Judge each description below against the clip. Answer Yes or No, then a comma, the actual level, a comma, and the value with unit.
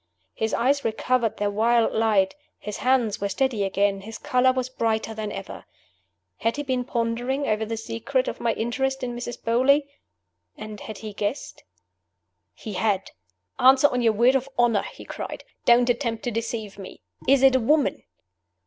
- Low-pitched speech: No, high, 230 Hz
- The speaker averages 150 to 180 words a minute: Yes, average, 170 wpm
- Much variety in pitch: No, average, 3.0 semitones